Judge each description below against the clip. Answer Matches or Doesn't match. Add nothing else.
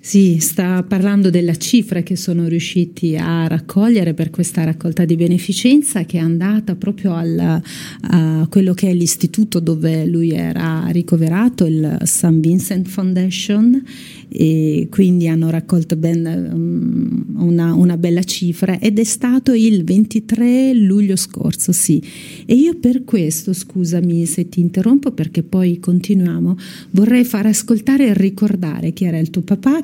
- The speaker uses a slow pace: Doesn't match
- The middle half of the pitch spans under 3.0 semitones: Doesn't match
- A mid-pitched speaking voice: Matches